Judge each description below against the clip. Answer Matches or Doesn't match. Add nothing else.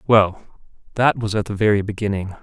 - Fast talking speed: Doesn't match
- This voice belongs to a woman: Doesn't match